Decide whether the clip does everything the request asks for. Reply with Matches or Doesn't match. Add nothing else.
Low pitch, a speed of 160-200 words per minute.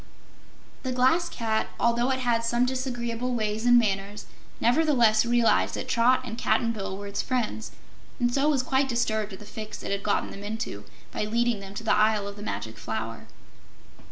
Doesn't match